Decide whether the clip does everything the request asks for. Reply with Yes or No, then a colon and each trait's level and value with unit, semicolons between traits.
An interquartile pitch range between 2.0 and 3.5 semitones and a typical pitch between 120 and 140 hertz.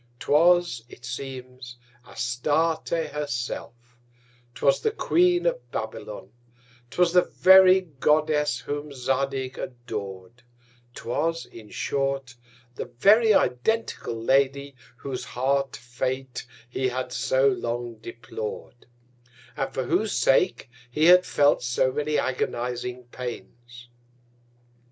No: average, 4.0 semitones; low, 135 Hz